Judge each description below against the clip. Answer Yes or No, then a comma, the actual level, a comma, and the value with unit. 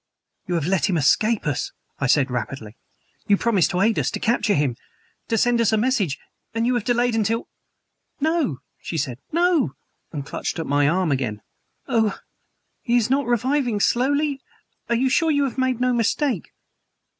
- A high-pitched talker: Yes, high, 225 Hz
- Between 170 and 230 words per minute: Yes, average, 180 wpm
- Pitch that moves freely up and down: Yes, wide, 7.8 semitones